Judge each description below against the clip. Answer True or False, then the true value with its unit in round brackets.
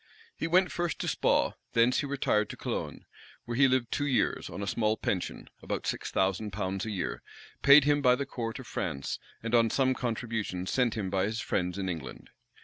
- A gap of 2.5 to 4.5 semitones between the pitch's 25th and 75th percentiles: False (5.1 semitones)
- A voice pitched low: True (115 Hz)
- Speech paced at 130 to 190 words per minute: False (205 wpm)